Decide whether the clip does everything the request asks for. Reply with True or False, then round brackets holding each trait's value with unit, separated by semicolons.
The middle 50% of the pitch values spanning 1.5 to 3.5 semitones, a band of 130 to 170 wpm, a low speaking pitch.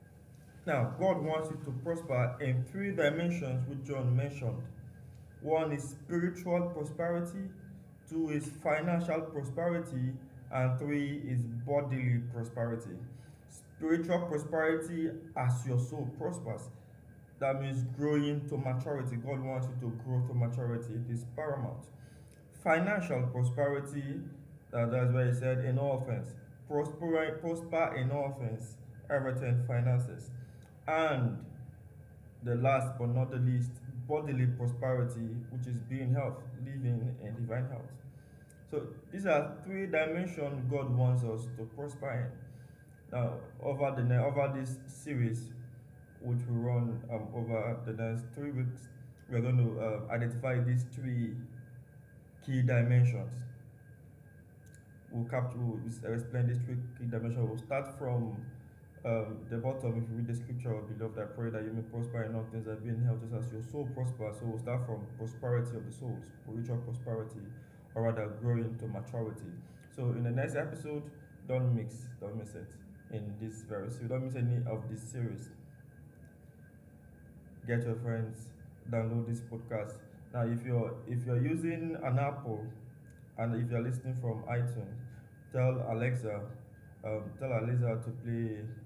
True (2.8 semitones; 145 wpm; 125 Hz)